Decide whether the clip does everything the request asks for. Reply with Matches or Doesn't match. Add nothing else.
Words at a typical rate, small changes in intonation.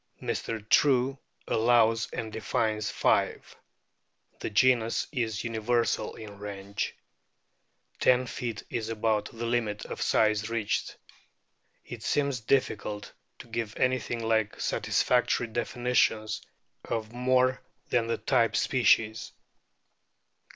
Doesn't match